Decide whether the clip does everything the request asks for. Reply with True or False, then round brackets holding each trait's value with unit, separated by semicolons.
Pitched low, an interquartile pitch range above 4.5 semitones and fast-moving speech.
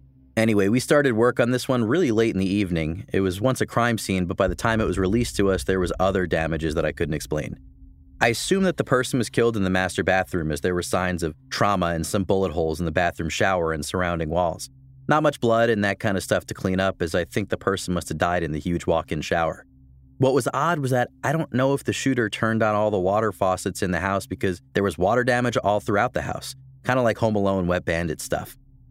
True (100 Hz; 5.4 semitones; 255 wpm)